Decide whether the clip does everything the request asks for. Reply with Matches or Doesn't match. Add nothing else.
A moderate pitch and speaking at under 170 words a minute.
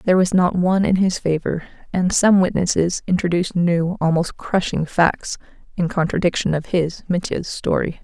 Matches